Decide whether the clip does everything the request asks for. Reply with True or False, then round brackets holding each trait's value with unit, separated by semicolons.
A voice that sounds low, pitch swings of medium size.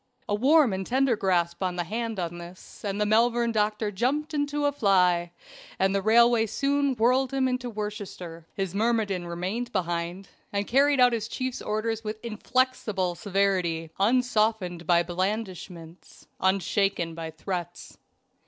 False (210 Hz; 4.8 semitones)